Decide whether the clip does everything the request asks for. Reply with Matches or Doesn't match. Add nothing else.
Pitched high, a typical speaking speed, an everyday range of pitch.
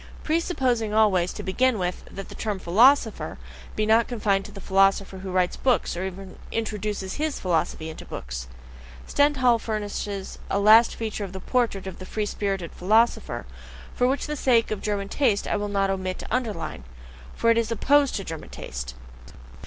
Matches